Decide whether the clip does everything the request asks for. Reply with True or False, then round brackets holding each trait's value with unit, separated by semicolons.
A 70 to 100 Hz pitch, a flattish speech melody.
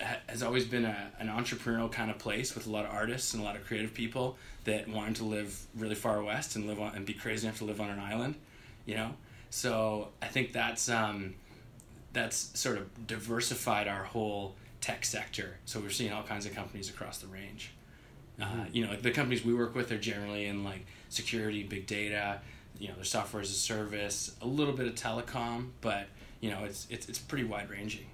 False (110 Hz; 2.3 semitones)